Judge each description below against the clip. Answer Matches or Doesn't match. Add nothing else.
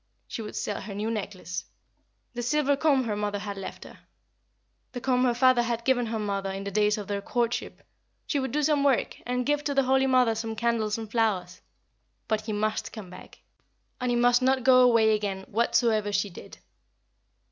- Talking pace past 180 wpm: Matches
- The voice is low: Doesn't match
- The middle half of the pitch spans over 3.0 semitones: Matches